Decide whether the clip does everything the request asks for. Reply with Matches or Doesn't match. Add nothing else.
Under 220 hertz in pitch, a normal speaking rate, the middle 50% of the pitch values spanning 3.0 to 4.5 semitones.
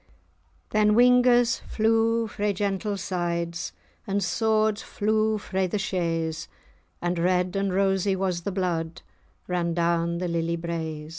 Doesn't match